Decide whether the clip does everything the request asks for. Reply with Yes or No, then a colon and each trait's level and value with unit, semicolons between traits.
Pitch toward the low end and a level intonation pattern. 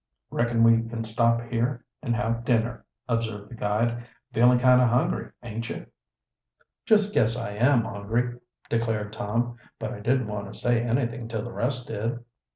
Yes: low, 115 Hz; narrow, 1.4 semitones